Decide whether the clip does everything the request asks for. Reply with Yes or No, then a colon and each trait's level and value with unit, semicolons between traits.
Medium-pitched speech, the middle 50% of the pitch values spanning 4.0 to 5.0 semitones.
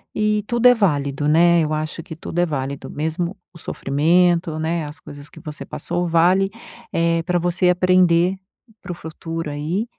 No: medium, 170 Hz; narrow, 2.5 semitones